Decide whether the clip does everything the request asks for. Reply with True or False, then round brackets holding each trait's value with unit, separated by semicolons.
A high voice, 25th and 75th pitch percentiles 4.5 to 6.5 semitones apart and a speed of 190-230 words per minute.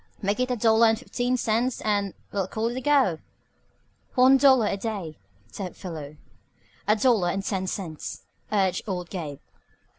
False (210 Hz; 4.8 semitones; 155 wpm)